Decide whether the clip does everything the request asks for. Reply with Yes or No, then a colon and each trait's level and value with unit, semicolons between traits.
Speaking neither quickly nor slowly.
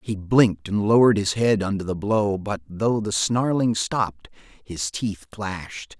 Yes: average, 170 wpm